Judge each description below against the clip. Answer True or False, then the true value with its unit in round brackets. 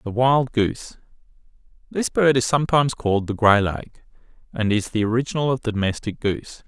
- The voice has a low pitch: True (120 Hz)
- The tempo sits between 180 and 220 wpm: False (160 wpm)